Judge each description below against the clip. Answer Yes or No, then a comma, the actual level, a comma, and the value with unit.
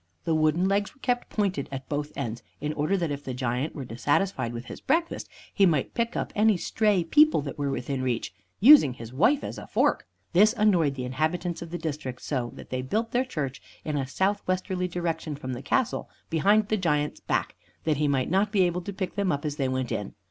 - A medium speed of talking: No, fast, 220 wpm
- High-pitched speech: No, medium, 160 Hz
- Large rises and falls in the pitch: Yes, wide, 6.4 semitones